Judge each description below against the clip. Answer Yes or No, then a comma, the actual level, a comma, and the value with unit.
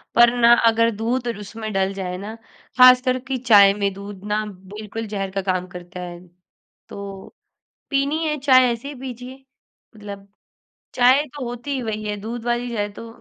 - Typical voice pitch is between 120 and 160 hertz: No, high, 220 Hz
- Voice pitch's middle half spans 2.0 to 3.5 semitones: No, average, 4.1 semitones